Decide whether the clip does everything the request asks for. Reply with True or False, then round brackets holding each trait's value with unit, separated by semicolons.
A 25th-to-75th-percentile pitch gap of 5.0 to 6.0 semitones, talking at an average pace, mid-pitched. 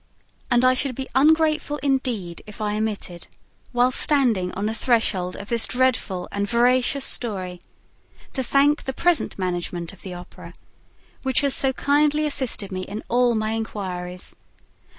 False (5.6 semitones; 155 wpm; 235 Hz)